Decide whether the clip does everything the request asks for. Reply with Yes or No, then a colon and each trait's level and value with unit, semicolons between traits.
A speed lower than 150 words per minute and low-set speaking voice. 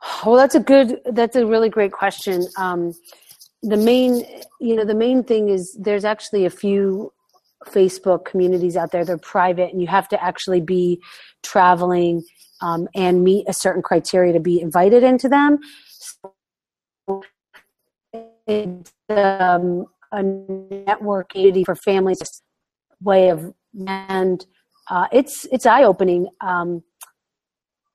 No: slow, 135 wpm; high, 195 Hz